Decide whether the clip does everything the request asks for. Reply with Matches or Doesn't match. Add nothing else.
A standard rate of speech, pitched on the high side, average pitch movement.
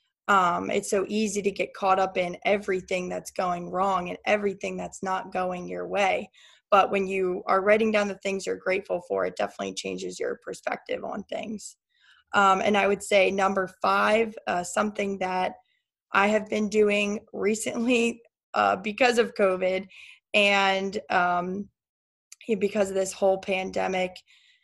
Doesn't match